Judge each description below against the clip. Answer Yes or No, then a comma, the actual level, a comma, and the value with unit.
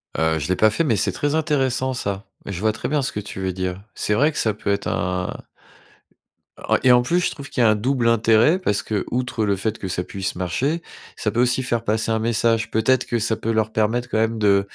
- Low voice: Yes, low, 110 Hz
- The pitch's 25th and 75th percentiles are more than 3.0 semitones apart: Yes, average, 3.6 semitones